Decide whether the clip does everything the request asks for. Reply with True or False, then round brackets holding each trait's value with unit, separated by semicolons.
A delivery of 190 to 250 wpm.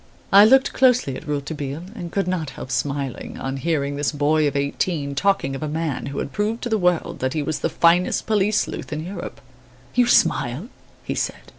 True (200 wpm)